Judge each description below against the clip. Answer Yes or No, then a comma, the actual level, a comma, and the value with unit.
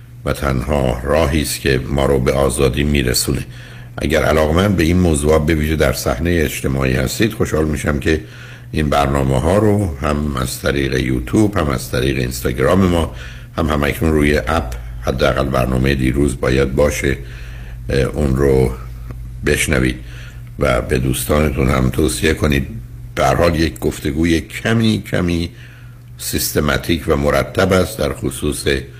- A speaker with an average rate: Yes, average, 135 wpm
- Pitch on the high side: No, very low, 75 Hz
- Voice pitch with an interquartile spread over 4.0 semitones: Yes, average, 4.5 semitones